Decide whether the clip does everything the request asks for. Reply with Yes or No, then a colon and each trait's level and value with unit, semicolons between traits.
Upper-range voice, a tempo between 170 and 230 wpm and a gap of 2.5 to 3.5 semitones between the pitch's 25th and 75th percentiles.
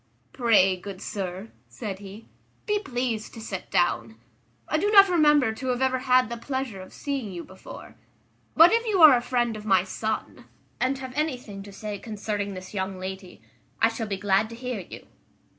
No: high, 220 Hz; average, 190 wpm; average, 4.9 semitones